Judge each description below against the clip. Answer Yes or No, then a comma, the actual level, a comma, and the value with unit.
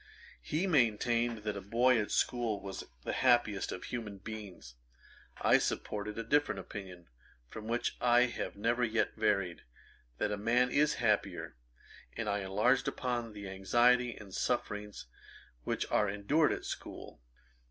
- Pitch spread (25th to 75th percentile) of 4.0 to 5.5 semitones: No, average, 3.2 semitones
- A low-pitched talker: Yes, low, 110 Hz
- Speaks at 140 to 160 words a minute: Yes, average, 145 wpm